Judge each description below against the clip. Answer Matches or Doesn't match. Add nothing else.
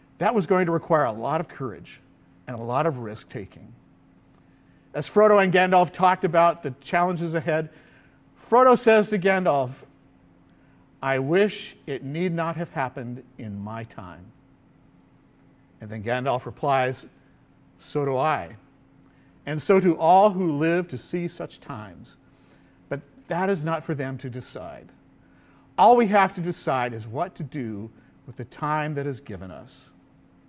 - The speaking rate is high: Doesn't match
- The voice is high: Doesn't match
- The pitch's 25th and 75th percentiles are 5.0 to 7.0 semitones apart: Matches